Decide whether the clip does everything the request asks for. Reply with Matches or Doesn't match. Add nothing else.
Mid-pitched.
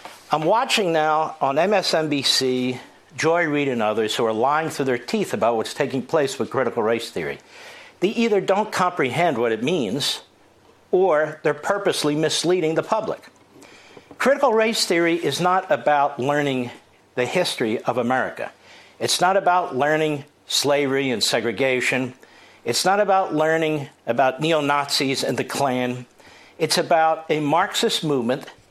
Matches